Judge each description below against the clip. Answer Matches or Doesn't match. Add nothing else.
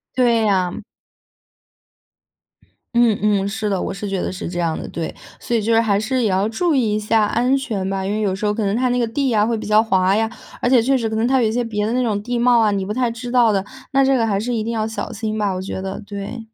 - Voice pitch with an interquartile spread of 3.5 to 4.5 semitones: Doesn't match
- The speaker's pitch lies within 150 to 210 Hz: Doesn't match